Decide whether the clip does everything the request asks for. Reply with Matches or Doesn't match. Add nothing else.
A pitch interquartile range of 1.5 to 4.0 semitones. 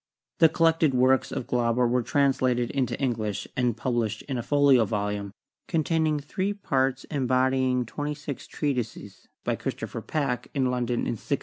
Matches